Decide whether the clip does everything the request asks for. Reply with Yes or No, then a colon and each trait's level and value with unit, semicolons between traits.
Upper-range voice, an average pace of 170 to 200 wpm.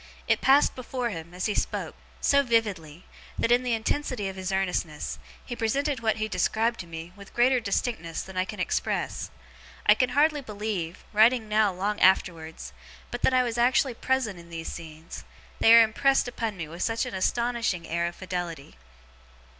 Yes: high, 215 Hz; average, 180 wpm